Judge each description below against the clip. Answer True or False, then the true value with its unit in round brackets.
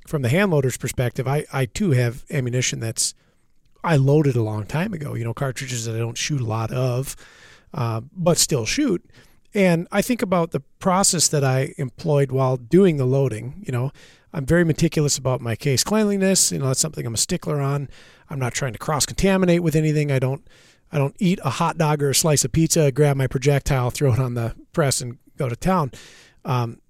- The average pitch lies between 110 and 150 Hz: True (140 Hz)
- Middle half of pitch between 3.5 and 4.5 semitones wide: True (4.1 semitones)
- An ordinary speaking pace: False (210 wpm)